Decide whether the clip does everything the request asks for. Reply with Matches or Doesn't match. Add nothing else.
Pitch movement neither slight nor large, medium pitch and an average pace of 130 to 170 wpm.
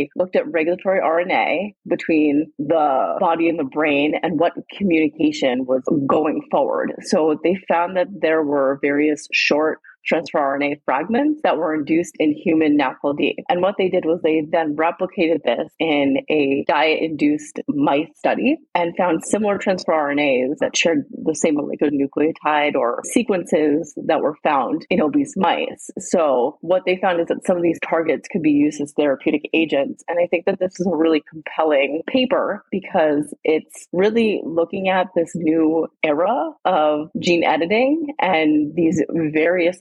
Matches